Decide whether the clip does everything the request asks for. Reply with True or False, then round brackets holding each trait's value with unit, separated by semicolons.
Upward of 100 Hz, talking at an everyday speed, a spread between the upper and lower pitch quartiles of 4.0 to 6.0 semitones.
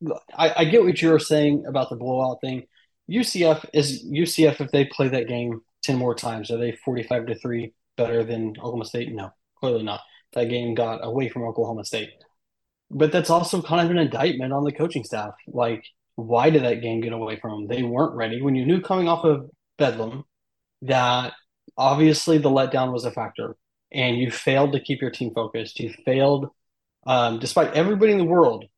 True (130 Hz; 195 wpm; 4.7 semitones)